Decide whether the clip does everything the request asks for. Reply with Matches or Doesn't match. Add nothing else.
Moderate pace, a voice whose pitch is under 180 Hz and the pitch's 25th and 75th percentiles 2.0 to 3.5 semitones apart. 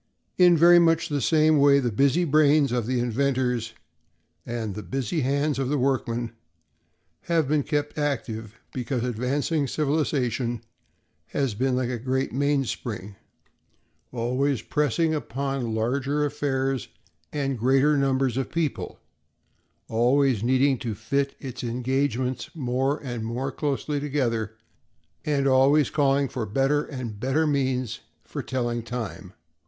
Doesn't match